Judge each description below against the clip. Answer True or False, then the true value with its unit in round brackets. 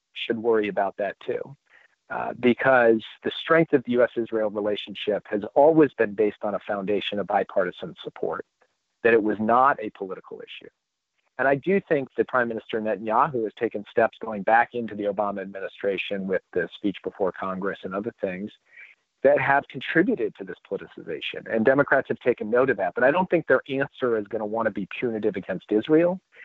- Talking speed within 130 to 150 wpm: False (190 wpm)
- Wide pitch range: True (7.7 semitones)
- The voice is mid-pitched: False (125 Hz)